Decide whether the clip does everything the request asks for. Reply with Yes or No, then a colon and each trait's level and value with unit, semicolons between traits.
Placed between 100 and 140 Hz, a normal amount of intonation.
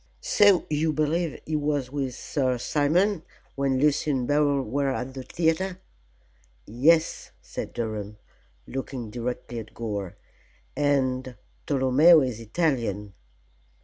Yes: low, 135 Hz; average, 3.8 semitones